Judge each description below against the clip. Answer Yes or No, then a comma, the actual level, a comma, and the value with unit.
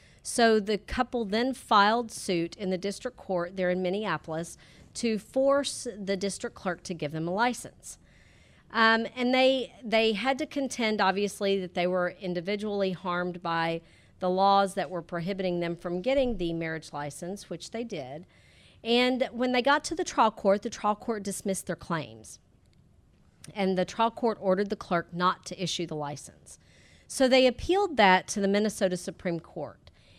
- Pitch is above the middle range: Yes, high, 195 Hz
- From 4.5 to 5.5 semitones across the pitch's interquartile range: Yes, average, 4.8 semitones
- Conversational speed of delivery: Yes, average, 170 wpm